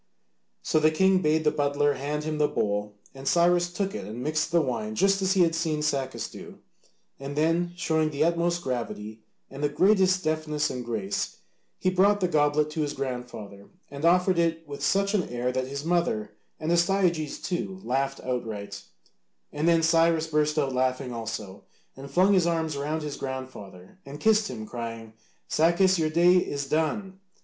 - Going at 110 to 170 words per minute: No, average, 180 wpm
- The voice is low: No, medium, 150 Hz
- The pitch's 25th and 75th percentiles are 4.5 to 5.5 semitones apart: Yes, average, 4.8 semitones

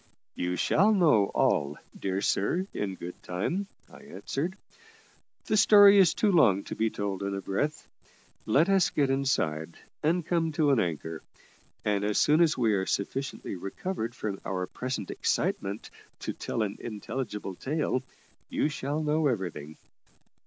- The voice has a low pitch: Yes, low, 120 Hz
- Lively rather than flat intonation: Yes, wide, 8.3 semitones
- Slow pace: No, average, 150 wpm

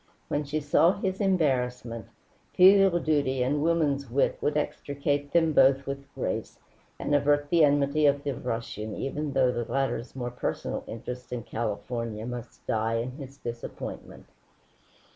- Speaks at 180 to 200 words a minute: No, average, 145 wpm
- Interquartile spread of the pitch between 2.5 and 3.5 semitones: Yes, average, 3.2 semitones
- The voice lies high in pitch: No, medium, 140 Hz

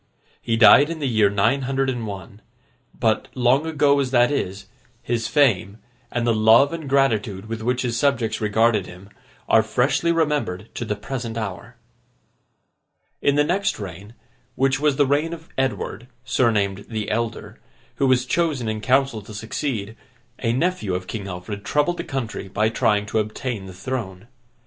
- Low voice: Yes, low, 115 Hz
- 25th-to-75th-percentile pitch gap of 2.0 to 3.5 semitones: No, average, 4.4 semitones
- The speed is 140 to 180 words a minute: Yes, average, 170 wpm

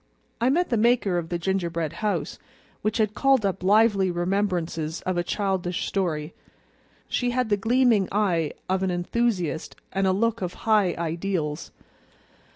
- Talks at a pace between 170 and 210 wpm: No, average, 155 wpm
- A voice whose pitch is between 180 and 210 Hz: Yes, high, 190 Hz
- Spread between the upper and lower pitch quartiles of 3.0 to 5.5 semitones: Yes, average, 3.9 semitones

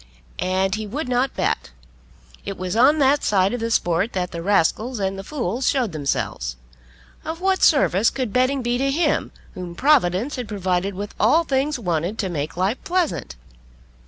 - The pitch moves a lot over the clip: Yes, wide, 6.5 semitones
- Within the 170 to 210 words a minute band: Yes, average, 175 wpm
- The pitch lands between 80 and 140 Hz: No, high, 220 Hz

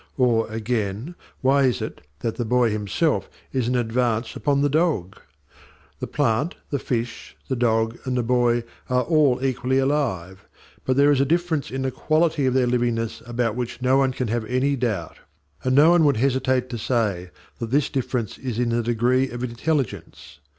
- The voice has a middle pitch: No, low, 125 Hz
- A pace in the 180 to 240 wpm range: Yes, average, 185 wpm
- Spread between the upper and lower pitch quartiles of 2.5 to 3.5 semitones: Yes, average, 2.8 semitones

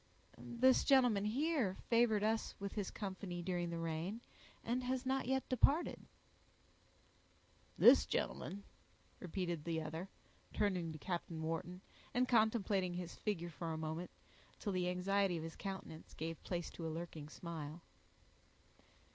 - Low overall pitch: No, medium, 185 Hz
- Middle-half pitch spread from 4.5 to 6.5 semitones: Yes, average, 4.8 semitones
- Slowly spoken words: Yes, slow, 130 wpm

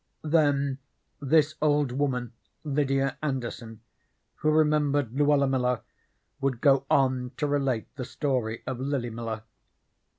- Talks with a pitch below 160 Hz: Yes, low, 135 Hz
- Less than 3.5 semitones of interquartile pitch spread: Yes, narrow, 2.6 semitones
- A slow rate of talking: Yes, slow, 120 wpm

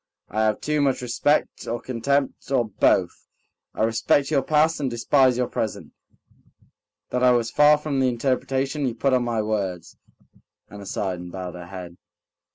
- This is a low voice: Yes, low, 120 Hz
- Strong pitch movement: No, average, 4.3 semitones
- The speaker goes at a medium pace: Yes, average, 165 wpm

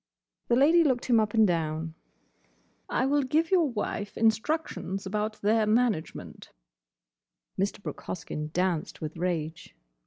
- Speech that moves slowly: Yes, slow, 130 wpm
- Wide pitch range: Yes, wide, 6.0 semitones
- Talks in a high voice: Yes, high, 215 Hz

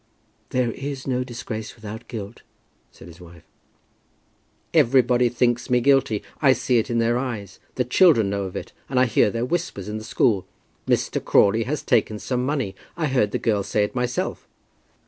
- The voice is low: Yes, low, 120 Hz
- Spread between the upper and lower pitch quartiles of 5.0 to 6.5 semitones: No, average, 3.2 semitones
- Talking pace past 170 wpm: Yes, average, 180 wpm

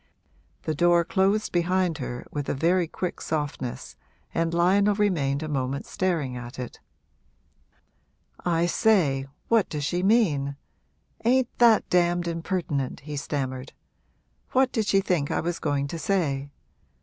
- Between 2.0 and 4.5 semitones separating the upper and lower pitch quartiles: No, average, 5.0 semitones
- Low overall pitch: No, medium, 170 Hz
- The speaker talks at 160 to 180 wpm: No, slow, 135 wpm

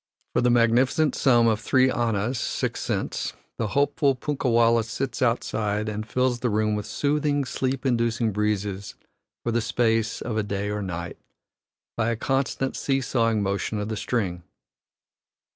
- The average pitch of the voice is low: Yes, low, 115 Hz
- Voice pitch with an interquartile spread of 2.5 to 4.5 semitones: Yes, average, 3.4 semitones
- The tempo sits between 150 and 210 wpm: Yes, average, 155 wpm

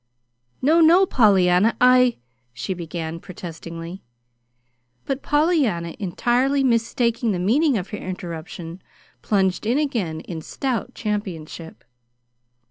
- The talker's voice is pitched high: Yes, high, 205 Hz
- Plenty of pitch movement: Yes, wide, 6.8 semitones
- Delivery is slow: Yes, slow, 110 wpm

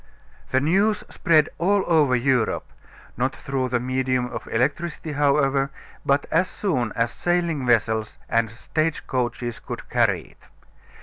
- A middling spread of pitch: Yes, average, 4.5 semitones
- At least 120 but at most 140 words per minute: Yes, slow, 135 wpm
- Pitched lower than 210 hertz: Yes, low, 135 Hz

